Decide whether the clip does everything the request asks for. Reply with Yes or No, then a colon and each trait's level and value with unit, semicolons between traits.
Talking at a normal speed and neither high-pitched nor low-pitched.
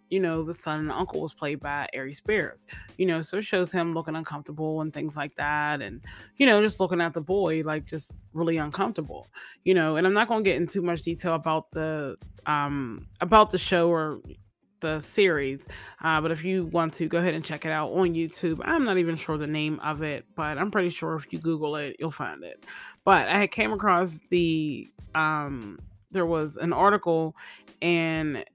No: fast, 210 wpm; medium, 160 Hz